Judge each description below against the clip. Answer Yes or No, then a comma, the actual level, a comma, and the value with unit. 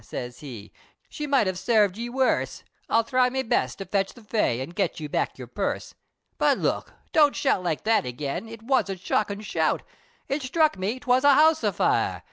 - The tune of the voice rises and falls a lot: Yes, wide, 6.2 semitones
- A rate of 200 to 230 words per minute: Yes, fast, 205 wpm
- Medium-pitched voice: No, high, 220 Hz